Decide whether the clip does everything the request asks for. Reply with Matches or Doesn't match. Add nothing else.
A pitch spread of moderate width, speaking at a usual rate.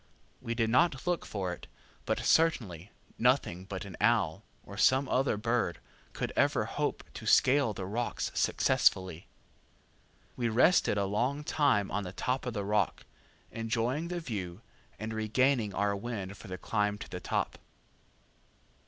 Matches